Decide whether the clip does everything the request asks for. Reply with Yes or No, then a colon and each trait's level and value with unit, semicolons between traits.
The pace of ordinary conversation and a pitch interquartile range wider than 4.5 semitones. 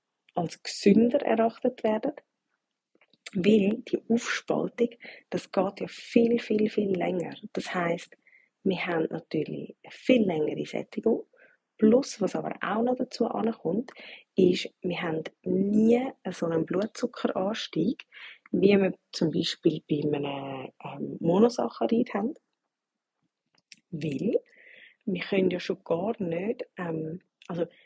No: slow, 120 wpm; average, 5.1 semitones